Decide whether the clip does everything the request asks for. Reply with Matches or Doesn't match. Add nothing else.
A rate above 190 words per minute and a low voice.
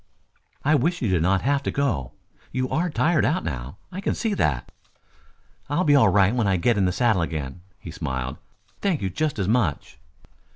Matches